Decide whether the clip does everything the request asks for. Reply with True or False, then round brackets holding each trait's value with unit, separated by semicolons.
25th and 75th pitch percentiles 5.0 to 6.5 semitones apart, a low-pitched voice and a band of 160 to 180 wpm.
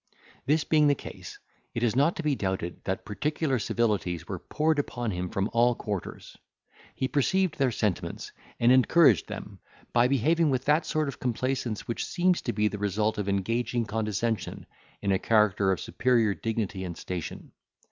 True (5.3 semitones; 115 Hz; 170 wpm)